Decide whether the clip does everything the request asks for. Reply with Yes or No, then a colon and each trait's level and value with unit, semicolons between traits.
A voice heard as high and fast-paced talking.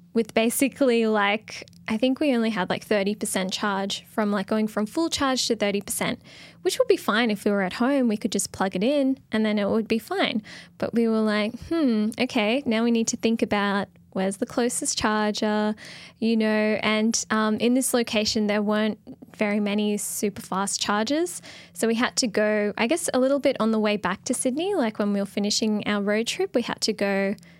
Yes: high, 220 Hz; fast, 215 wpm